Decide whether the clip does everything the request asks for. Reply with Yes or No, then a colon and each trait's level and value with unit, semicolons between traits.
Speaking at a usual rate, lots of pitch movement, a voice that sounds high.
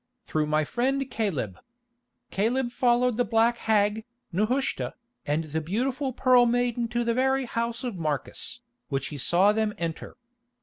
Yes: average, 145 wpm; wide, 6.2 semitones; high, 230 Hz